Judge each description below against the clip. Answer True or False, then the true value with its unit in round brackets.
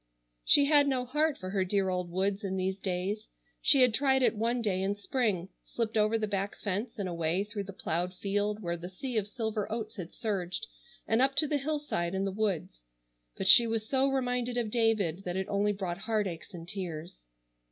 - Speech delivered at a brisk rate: True (210 wpm)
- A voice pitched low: False (205 Hz)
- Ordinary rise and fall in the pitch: True (4.1 semitones)